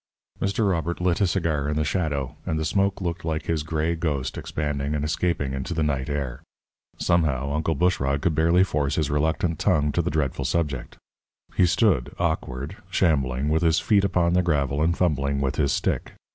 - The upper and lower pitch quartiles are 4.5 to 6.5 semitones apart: No, average, 3.3 semitones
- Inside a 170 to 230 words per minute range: Yes, average, 185 wpm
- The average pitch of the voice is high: No, very low, 80 Hz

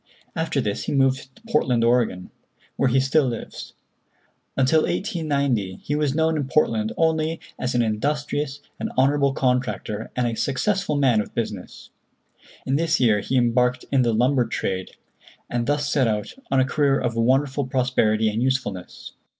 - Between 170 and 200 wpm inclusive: No, average, 160 wpm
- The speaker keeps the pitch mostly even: No, average, 3.7 semitones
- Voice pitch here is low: Yes, low, 130 Hz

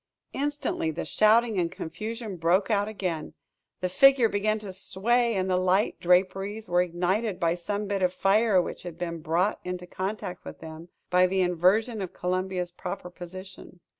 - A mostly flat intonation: No, average, 3.0 semitones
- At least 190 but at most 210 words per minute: No, average, 165 wpm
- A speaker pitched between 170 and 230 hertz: Yes, medium, 185 Hz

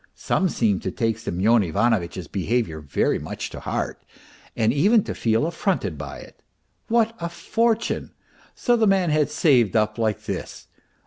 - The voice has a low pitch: Yes, low, 115 Hz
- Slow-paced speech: No, average, 155 wpm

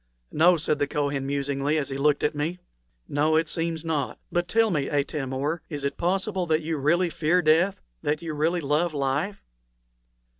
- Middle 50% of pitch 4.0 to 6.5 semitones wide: No, average, 2.9 semitones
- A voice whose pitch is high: No, medium, 155 Hz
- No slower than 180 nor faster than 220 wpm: Yes, average, 185 wpm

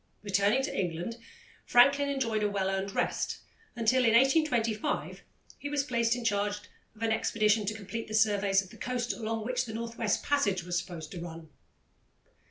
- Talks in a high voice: Yes, high, 220 Hz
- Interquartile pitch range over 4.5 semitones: No, average, 3.4 semitones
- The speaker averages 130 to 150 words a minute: No, average, 180 wpm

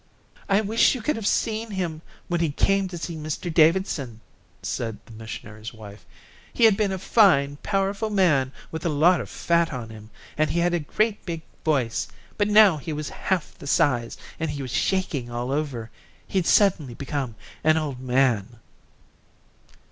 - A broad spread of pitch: Yes, wide, 6.7 semitones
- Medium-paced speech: Yes, average, 175 wpm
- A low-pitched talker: No, medium, 155 Hz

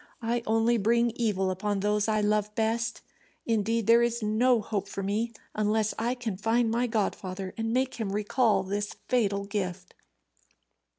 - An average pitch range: No, narrow, 2.3 semitones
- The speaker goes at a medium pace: Yes, average, 160 wpm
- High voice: Yes, high, 215 Hz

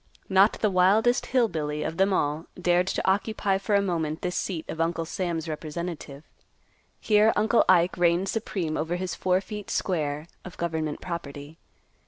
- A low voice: No, medium, 175 Hz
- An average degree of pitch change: Yes, average, 3.4 semitones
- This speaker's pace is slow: No, average, 165 wpm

